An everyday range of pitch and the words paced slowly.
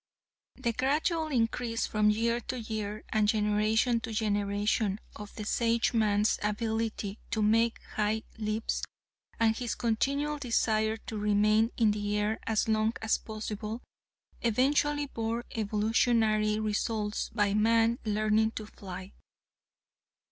No: narrow, 1.6 semitones; slow, 120 wpm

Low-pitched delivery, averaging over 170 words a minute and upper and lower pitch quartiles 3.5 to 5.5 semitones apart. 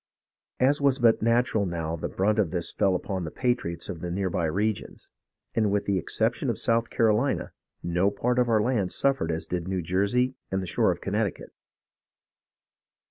Yes: low, 100 Hz; average, 185 wpm; average, 5.0 semitones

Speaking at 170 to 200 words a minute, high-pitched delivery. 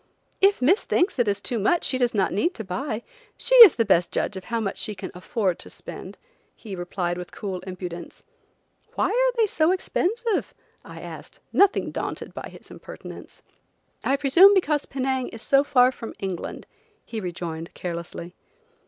Yes: average, 175 wpm; high, 230 Hz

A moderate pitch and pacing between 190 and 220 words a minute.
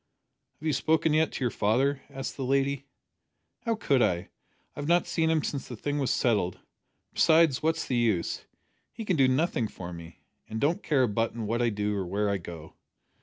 No: low, 130 Hz; average, 200 wpm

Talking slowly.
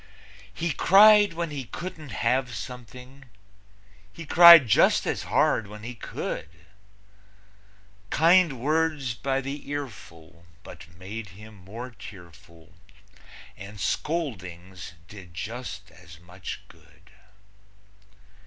Yes: slow, 105 wpm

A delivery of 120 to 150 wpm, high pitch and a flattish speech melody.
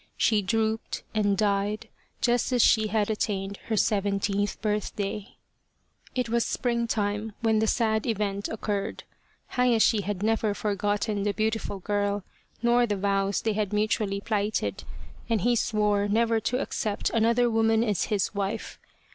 Yes: average, 140 wpm; high, 215 Hz; narrow, 1.7 semitones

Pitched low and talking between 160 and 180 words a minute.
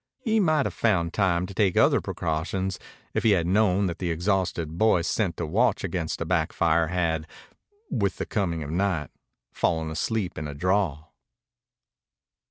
Yes: very low, 90 Hz; average, 170 wpm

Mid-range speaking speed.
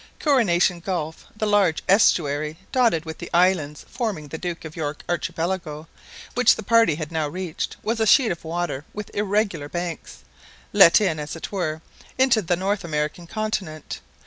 Yes: average, 165 wpm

